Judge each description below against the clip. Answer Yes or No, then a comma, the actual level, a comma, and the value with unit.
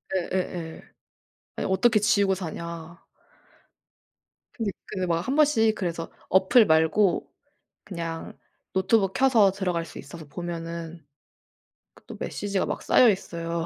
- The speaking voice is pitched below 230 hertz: Yes, medium, 185 Hz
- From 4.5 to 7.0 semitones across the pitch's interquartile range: No, average, 3.5 semitones